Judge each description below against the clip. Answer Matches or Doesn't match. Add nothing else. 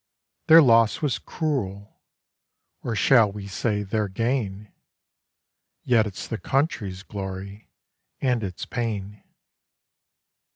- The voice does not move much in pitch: Doesn't match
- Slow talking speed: Matches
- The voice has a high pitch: Doesn't match